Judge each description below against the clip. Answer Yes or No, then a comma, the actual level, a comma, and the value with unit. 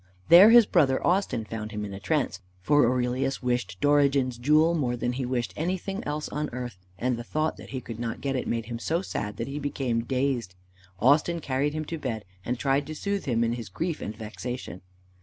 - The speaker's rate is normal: No, fast, 215 wpm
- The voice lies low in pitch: Yes, low, 130 Hz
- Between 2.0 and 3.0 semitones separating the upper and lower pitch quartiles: No, average, 4.3 semitones